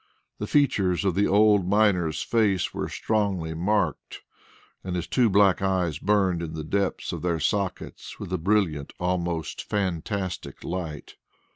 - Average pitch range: Yes, average, 3.3 semitones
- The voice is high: No, very low, 95 Hz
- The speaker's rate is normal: Yes, average, 145 wpm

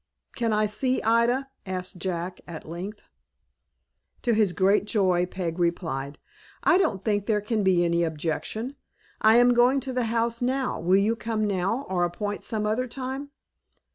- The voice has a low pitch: No, high, 210 Hz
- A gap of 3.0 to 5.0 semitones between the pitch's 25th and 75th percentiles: Yes, average, 4.7 semitones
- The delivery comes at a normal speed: Yes, average, 165 wpm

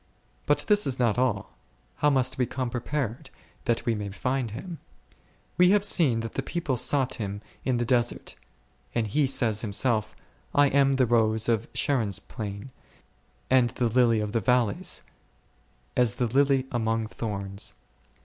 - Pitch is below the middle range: Yes, low, 120 Hz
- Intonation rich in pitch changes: No, average, 3.3 semitones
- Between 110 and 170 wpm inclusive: Yes, average, 160 wpm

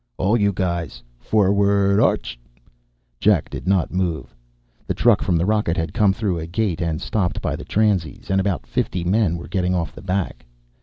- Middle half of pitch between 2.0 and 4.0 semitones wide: Yes, average, 2.9 semitones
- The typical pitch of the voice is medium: No, very low, 95 Hz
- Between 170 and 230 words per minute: Yes, average, 185 wpm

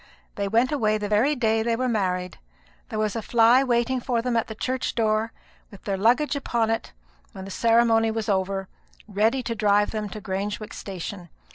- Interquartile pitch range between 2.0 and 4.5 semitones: Yes, narrow, 2.5 semitones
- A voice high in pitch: Yes, high, 220 Hz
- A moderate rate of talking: Yes, average, 190 wpm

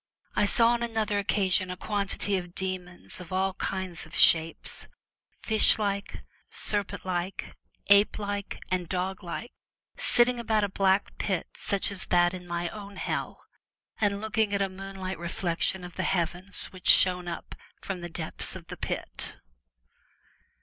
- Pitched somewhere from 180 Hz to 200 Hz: Yes, high, 190 Hz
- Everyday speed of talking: Yes, average, 165 wpm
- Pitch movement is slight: Yes, narrow, 2.2 semitones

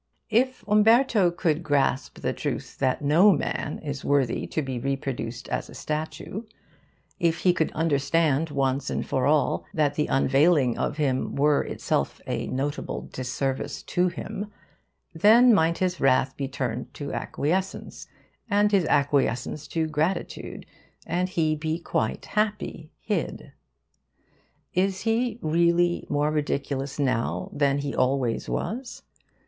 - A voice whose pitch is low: No, medium, 155 Hz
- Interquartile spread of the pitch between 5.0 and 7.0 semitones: No, average, 4.6 semitones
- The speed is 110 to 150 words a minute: Yes, slow, 135 wpm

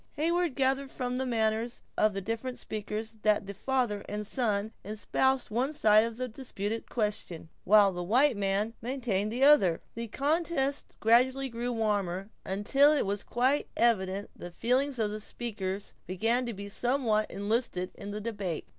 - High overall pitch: Yes, high, 225 Hz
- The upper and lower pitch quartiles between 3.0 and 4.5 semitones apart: Yes, average, 4.0 semitones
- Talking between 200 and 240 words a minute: No, average, 165 wpm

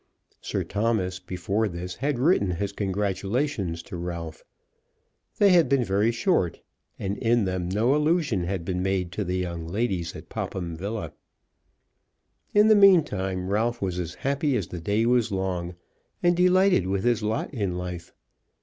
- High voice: No, low, 100 Hz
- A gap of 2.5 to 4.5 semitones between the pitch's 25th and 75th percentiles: No, average, 5.2 semitones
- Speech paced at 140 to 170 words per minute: Yes, average, 160 wpm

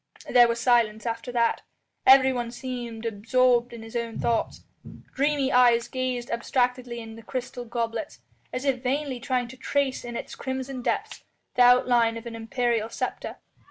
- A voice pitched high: Yes, high, 245 Hz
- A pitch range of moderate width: No, narrow, 1.7 semitones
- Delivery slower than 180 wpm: Yes, average, 155 wpm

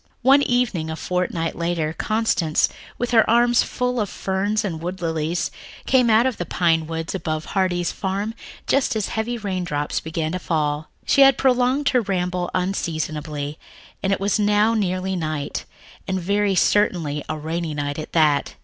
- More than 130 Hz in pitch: Yes, medium, 185 Hz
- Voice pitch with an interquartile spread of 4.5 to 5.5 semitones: Yes, average, 5.2 semitones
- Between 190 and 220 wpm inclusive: No, average, 165 wpm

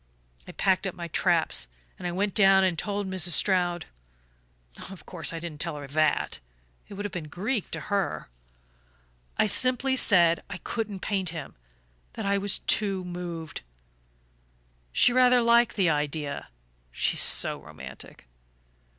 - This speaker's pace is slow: No, average, 145 wpm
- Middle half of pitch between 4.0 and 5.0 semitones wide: No, average, 3.6 semitones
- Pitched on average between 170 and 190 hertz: Yes, medium, 185 Hz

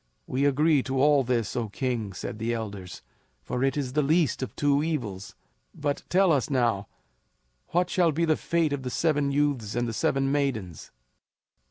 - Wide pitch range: No, average, 4.1 semitones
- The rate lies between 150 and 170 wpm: No, average, 180 wpm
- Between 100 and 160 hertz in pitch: Yes, low, 135 Hz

